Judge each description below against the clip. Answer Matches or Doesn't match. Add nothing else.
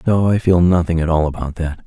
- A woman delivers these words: Doesn't match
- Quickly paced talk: Matches